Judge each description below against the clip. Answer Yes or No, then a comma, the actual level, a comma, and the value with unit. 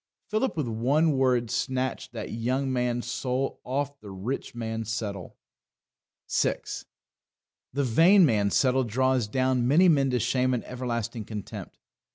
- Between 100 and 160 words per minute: Yes, average, 140 wpm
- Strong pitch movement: No, average, 2.8 semitones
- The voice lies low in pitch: Yes, low, 125 Hz